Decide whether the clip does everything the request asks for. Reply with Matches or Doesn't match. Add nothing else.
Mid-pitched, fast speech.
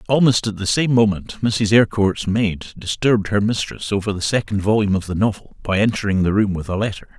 Doesn't match